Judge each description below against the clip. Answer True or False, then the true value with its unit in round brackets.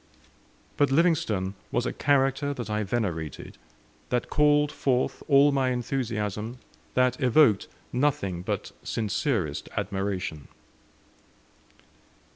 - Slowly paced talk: True (95 wpm)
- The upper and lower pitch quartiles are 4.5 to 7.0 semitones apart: True (5.2 semitones)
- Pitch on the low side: True (120 Hz)